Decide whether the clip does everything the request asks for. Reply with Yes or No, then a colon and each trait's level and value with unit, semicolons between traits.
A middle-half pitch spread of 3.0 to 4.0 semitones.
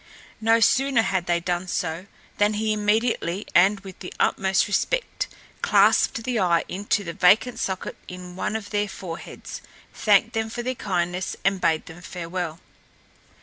Yes: average, 3.7 semitones